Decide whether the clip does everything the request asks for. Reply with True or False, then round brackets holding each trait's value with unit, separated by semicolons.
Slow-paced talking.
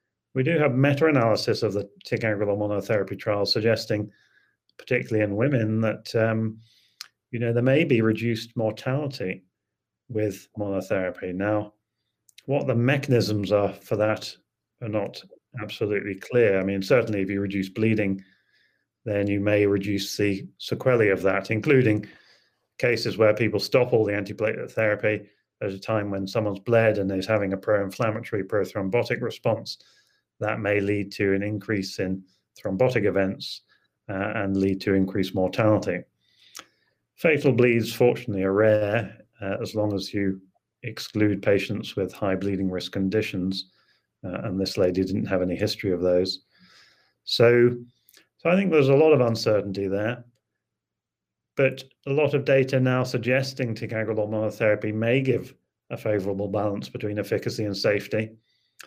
False (145 wpm)